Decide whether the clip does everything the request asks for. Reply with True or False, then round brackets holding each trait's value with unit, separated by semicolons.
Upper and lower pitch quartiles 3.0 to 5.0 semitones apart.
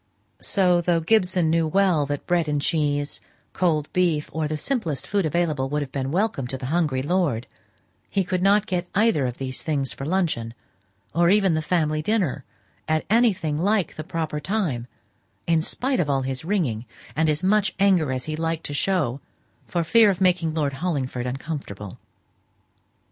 True (4.3 semitones)